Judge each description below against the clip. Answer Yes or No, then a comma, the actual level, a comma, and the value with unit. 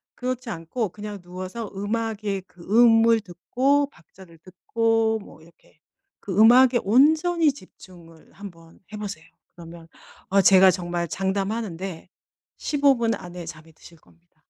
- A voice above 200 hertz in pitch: No, high, 195 Hz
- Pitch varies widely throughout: No, average, 4.9 semitones